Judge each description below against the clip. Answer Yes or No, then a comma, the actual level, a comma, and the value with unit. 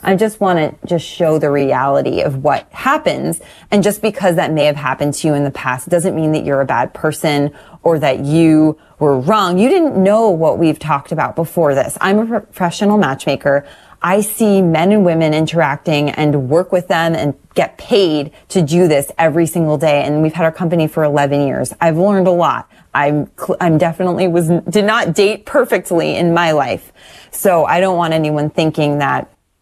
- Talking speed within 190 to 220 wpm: Yes, average, 195 wpm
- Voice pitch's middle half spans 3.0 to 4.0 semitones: Yes, average, 3.7 semitones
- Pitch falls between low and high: Yes, medium, 165 Hz